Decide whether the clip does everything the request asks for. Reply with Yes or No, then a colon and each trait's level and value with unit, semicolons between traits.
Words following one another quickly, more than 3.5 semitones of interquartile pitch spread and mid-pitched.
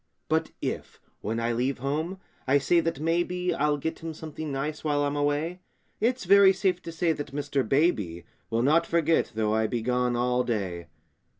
No: average, 185 wpm; average, 5.1 semitones; medium, 145 Hz